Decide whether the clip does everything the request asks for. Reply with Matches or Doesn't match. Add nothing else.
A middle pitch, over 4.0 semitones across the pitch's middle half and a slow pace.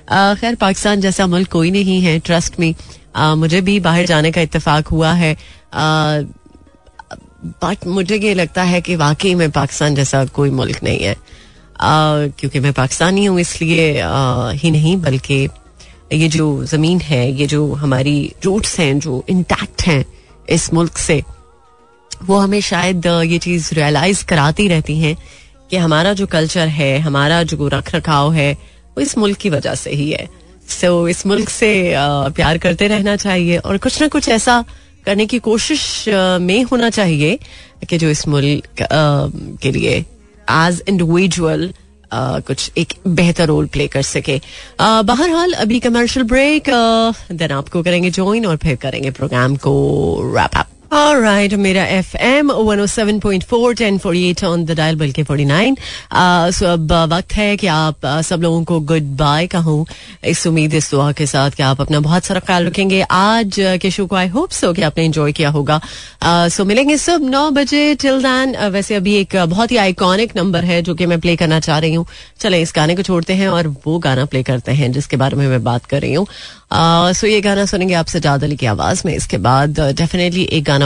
Doesn't match